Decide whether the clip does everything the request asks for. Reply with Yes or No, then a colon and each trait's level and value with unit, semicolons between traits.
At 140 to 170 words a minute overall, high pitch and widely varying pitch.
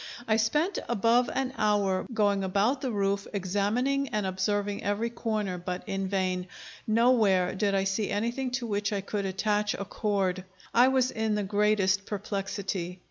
No: average, 160 wpm; high, 205 Hz; average, 2.7 semitones